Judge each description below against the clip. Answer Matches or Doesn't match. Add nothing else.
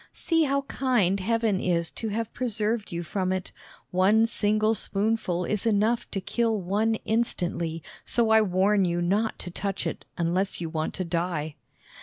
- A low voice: Doesn't match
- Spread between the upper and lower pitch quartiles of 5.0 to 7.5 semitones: Doesn't match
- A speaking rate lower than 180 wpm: Matches